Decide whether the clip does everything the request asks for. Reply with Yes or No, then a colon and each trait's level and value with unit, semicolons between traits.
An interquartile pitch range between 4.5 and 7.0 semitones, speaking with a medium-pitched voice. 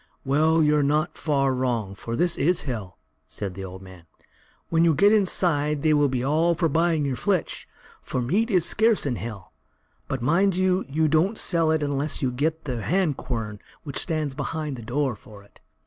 Yes: average, 4.9 semitones; medium, 150 Hz